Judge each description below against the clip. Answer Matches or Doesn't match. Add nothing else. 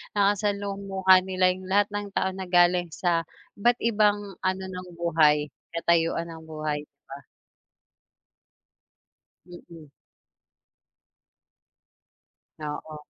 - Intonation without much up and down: Doesn't match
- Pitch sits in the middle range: Matches